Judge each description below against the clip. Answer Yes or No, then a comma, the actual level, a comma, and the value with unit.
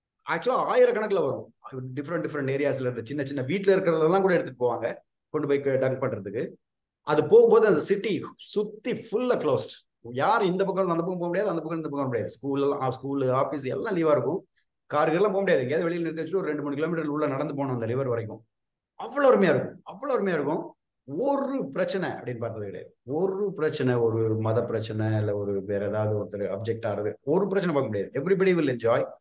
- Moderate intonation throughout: No, wide, 7.2 semitones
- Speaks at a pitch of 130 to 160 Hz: Yes, medium, 140 Hz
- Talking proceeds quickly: Yes, fast, 185 wpm